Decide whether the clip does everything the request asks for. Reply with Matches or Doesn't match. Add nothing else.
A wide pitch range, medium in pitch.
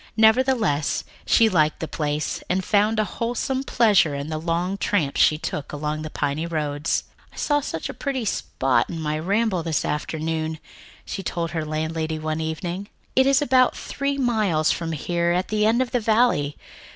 Matches